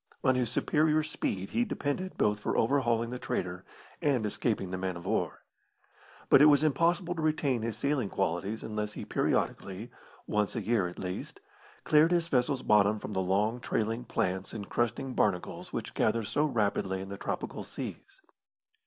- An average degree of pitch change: No, wide, 6.4 semitones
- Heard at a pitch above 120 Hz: No, low, 115 Hz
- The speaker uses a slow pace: No, average, 175 wpm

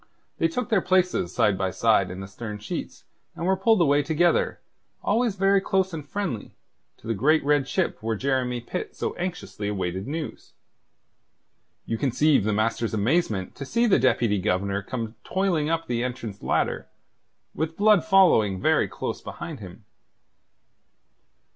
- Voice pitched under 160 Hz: Yes, low, 135 Hz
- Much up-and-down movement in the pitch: Yes, wide, 8.8 semitones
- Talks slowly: No, average, 155 wpm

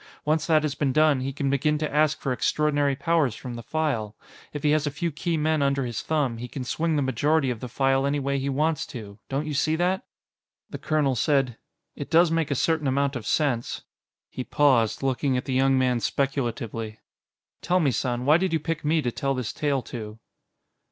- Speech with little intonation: No, average, 3.2 semitones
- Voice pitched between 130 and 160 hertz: Yes, medium, 140 Hz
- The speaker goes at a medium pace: No, fast, 215 wpm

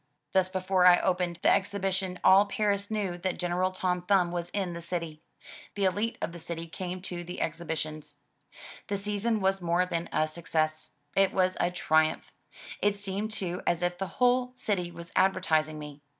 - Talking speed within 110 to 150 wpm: No, average, 180 wpm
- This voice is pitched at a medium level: Yes, medium, 180 Hz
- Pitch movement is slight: Yes, narrow, 2.3 semitones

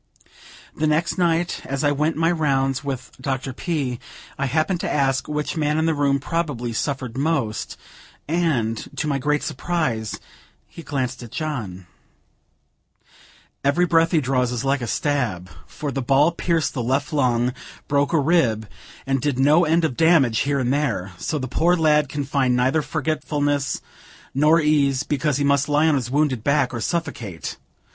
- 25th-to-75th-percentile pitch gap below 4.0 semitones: Yes, average, 3.3 semitones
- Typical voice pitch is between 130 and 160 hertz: Yes, medium, 140 Hz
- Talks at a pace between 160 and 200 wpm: Yes, average, 170 wpm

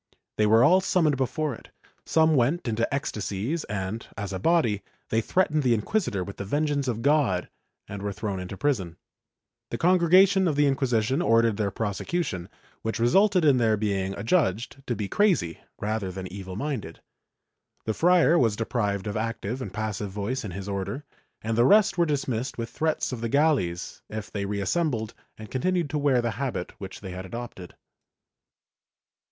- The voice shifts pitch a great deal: Yes, wide, 6.5 semitones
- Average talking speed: Yes, average, 170 wpm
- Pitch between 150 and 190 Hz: No, low, 115 Hz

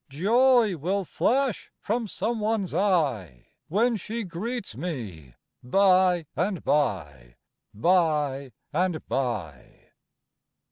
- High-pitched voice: No, medium, 175 Hz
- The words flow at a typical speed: No, slow, 95 wpm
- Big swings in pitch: Yes, wide, 7.8 semitones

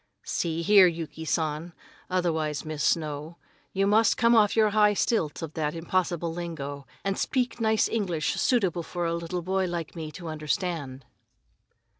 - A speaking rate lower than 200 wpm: Yes, average, 155 wpm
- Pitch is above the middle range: No, medium, 170 Hz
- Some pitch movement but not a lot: Yes, average, 3.8 semitones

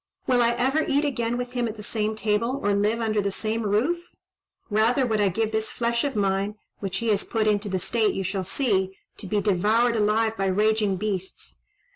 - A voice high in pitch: Yes, high, 215 Hz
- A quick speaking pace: Yes, fast, 210 wpm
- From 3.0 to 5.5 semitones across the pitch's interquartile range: No, narrow, 2.5 semitones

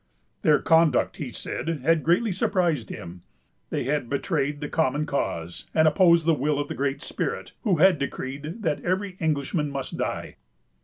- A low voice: No, medium, 150 Hz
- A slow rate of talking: No, average, 165 wpm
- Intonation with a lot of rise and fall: No, average, 3.2 semitones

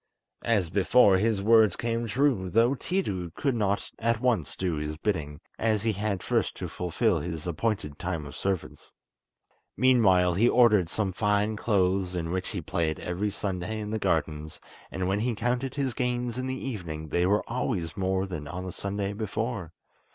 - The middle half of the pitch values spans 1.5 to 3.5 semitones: No, average, 4.3 semitones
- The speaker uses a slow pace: No, average, 175 wpm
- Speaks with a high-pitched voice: No, low, 100 Hz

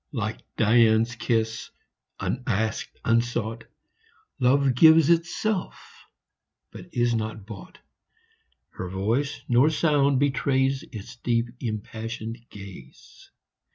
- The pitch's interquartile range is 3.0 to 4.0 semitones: Yes, average, 3.5 semitones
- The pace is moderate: No, slow, 95 wpm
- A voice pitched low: Yes, low, 120 Hz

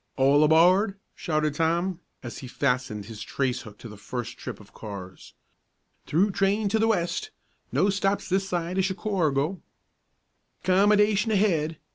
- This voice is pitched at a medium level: Yes, medium, 170 Hz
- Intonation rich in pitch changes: Yes, wide, 6.3 semitones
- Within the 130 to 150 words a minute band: Yes, average, 145 wpm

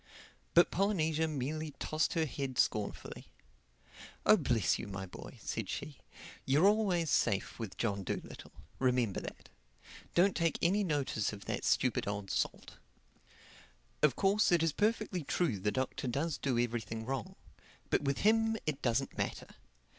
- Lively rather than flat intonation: Yes, wide, 6.6 semitones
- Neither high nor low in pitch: Yes, medium, 145 Hz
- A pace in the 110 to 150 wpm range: Yes, average, 145 wpm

